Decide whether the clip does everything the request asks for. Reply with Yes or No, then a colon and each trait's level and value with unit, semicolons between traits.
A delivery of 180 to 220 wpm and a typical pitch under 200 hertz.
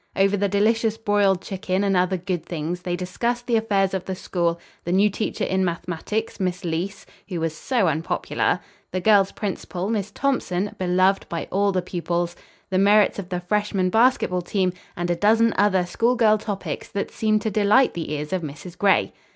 Yes: average, 185 wpm; high, 190 Hz